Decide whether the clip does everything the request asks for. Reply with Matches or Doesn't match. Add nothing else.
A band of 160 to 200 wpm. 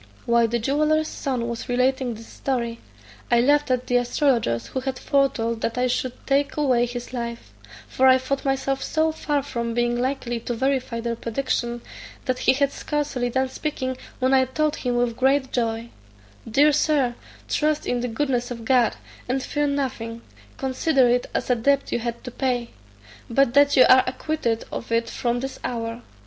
Matches